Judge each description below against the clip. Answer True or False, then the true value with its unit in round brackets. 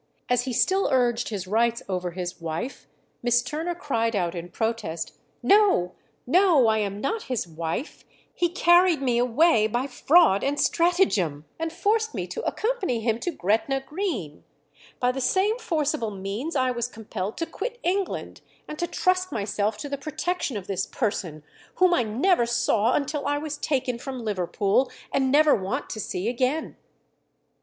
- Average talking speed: True (165 wpm)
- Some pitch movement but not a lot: False (7.6 semitones)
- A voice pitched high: True (250 Hz)